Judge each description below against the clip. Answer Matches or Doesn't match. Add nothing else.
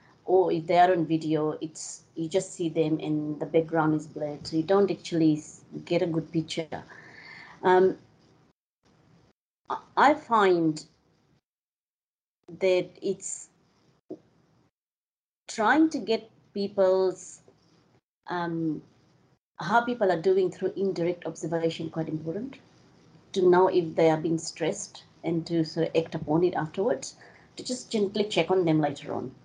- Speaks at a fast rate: Doesn't match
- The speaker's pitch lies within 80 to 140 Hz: Doesn't match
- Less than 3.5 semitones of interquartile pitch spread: Matches